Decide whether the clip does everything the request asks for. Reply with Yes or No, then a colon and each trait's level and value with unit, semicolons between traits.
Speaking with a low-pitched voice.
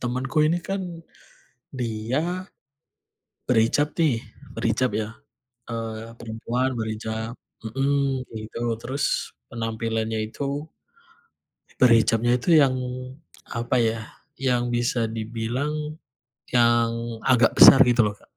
Yes: low, 120 Hz